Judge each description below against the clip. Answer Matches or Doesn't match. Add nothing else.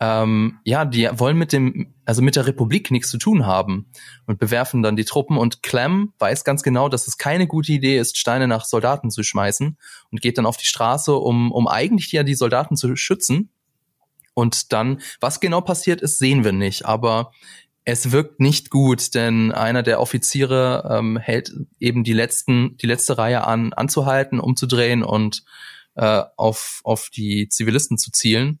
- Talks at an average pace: Matches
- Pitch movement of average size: Matches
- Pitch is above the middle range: Doesn't match